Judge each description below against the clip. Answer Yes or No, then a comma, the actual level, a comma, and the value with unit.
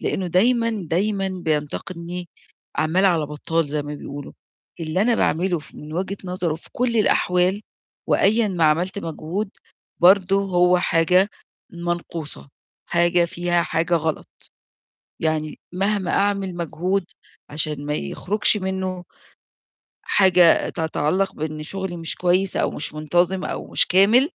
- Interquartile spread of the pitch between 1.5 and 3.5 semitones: Yes, average, 3.1 semitones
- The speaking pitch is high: No, medium, 175 Hz